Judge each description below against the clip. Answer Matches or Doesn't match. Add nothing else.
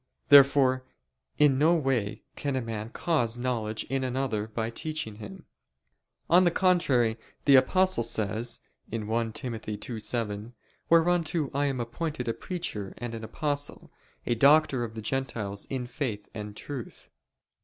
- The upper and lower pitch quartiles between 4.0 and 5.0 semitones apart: Matches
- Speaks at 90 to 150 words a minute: Matches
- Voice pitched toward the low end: Matches